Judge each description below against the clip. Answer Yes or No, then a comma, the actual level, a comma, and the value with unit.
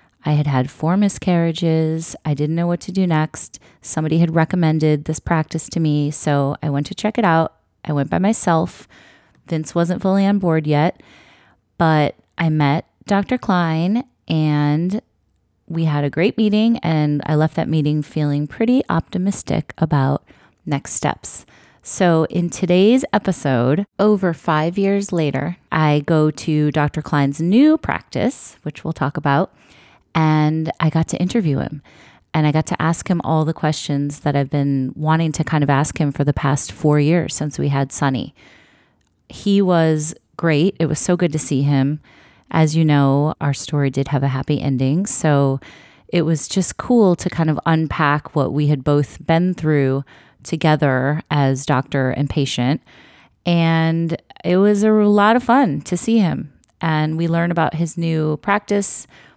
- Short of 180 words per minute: Yes, average, 170 wpm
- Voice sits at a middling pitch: Yes, medium, 160 Hz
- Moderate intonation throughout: Yes, average, 3.0 semitones